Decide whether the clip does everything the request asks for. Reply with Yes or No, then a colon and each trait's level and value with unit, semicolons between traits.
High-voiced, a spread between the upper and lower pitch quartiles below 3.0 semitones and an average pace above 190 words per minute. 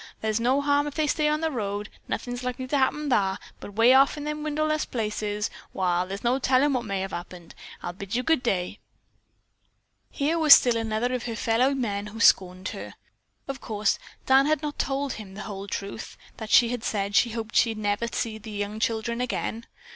No: high, 230 Hz; average, 4.7 semitones; fast, 205 wpm